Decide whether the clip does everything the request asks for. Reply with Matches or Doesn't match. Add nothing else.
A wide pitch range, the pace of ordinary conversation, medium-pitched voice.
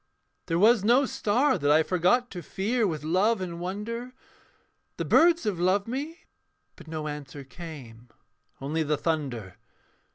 Matches